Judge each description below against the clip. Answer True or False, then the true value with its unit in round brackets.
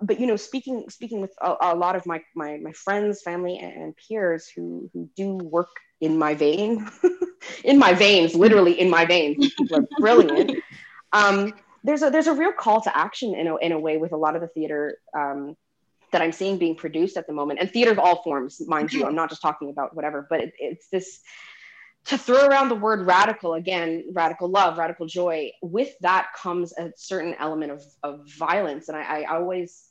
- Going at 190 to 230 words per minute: True (205 wpm)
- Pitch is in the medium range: True (175 Hz)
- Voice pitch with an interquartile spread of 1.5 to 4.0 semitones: False (4.6 semitones)